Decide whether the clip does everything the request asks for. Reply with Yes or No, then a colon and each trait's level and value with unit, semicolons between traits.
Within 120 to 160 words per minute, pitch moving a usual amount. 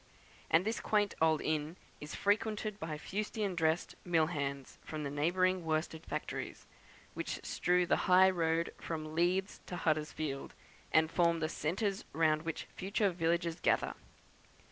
Yes: average, 145 wpm; average, 3.0 semitones